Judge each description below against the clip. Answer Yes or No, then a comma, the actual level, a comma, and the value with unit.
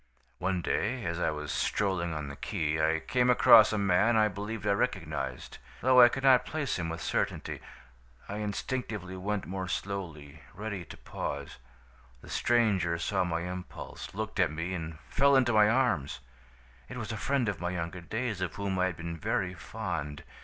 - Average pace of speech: Yes, average, 180 wpm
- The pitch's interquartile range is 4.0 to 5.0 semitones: Yes, average, 4.7 semitones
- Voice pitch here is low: Yes, very low, 95 Hz